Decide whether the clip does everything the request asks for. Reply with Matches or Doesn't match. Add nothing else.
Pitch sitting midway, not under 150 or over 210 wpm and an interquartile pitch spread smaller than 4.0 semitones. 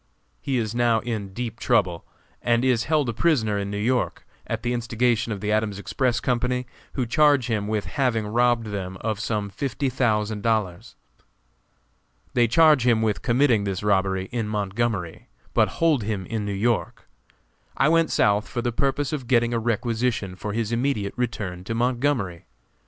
Doesn't match